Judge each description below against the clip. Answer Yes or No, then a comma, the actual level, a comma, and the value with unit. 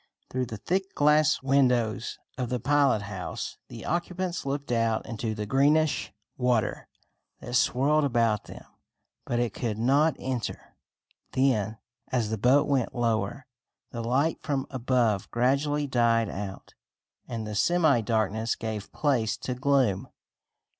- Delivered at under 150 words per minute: Yes, slow, 135 wpm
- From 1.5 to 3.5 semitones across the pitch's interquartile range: No, average, 3.9 semitones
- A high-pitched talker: No, low, 125 Hz